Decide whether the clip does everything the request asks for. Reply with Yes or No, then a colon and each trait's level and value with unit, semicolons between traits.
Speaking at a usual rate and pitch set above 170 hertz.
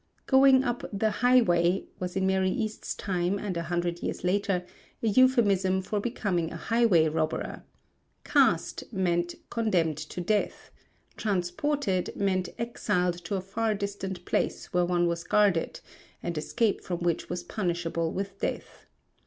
Yes: average, 145 wpm; high, 190 Hz